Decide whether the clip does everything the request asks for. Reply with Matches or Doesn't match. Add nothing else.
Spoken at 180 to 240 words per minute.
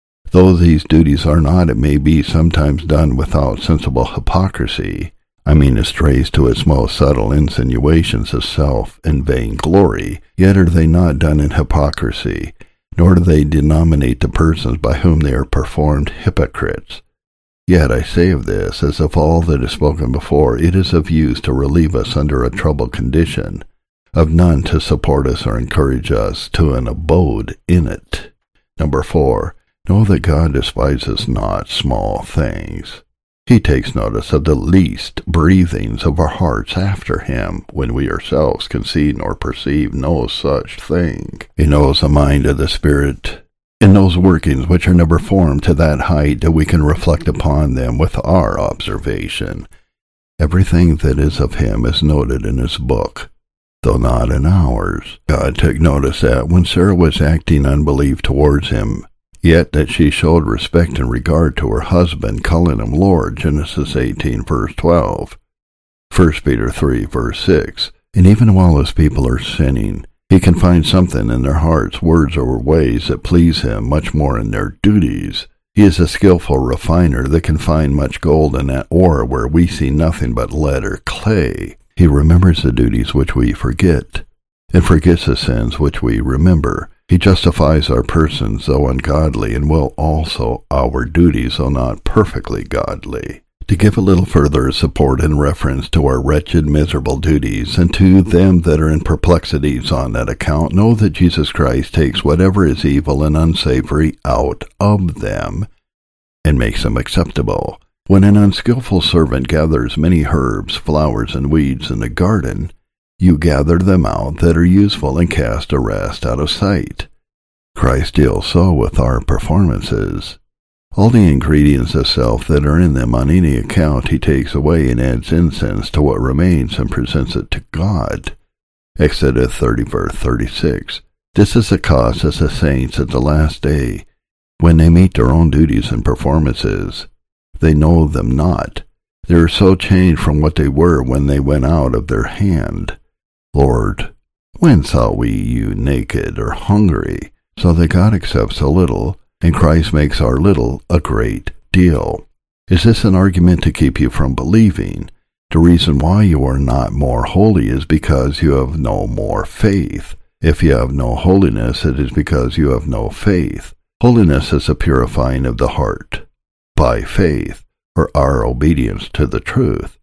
Doesn't match